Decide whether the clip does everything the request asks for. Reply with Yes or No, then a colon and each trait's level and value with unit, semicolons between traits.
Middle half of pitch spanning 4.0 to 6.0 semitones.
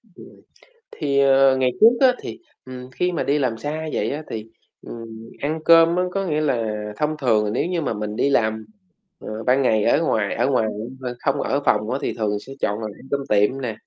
Yes: average, 5.2 semitones